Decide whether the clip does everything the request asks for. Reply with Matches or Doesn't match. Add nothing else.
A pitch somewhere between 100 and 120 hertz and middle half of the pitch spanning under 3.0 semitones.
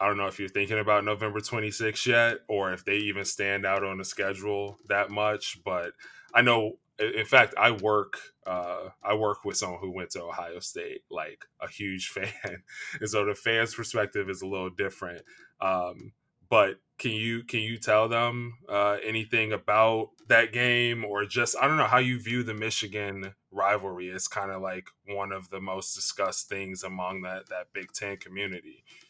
Matches